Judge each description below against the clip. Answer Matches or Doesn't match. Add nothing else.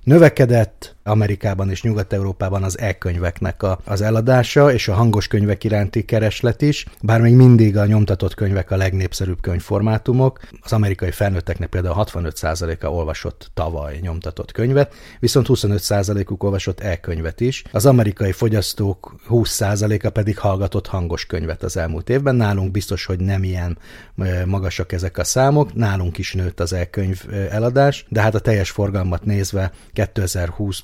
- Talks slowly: Doesn't match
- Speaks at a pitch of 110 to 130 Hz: Doesn't match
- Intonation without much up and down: Doesn't match